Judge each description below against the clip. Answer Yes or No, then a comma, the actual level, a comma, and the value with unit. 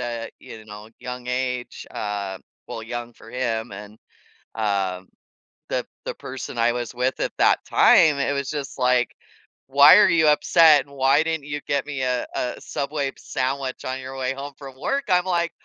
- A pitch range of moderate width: Yes, average, 3.1 semitones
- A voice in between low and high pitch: No, low, 130 Hz